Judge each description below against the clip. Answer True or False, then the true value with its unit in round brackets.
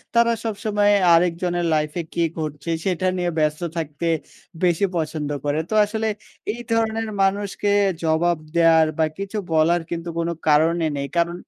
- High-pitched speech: False (170 Hz)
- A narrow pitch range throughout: False (4.0 semitones)